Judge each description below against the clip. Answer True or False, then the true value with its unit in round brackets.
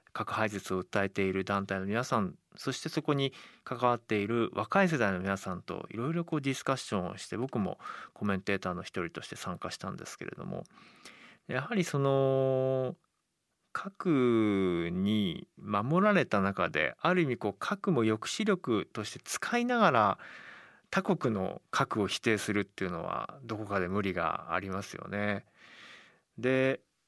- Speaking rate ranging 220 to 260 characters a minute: False (305 characters per minute)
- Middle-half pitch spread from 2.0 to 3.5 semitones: False (6.3 semitones)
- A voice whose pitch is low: True (115 Hz)